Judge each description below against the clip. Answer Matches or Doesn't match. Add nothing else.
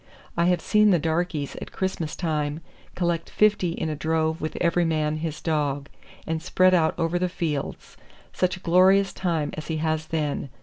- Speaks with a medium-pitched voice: Matches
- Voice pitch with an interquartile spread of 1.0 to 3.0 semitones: Matches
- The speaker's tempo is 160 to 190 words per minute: Matches